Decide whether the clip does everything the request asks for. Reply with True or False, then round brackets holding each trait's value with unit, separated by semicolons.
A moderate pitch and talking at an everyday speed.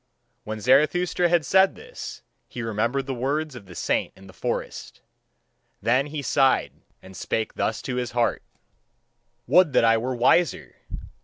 False (130 Hz; 155 wpm)